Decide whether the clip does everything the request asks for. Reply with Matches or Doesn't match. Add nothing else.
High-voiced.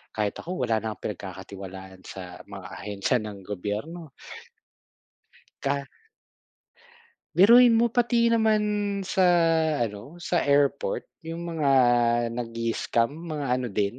Doesn't match